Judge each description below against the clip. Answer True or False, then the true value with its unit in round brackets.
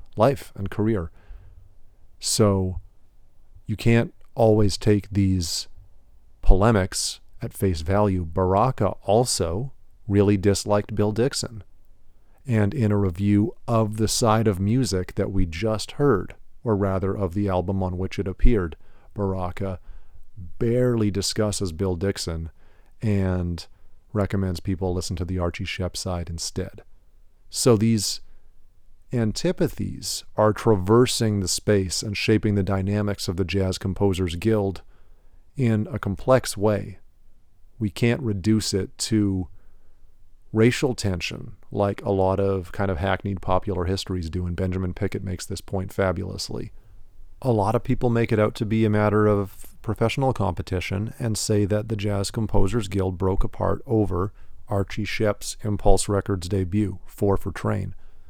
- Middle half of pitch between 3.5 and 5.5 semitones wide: False (2.4 semitones)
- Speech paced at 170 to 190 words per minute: False (135 wpm)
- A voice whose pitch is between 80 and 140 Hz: True (100 Hz)